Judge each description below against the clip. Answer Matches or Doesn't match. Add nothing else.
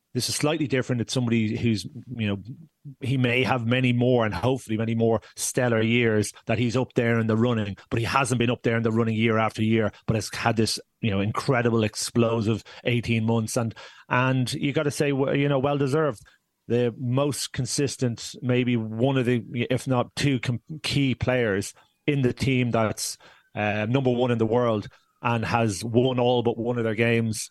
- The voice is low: Matches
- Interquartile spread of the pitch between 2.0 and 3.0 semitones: Matches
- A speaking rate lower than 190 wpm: Doesn't match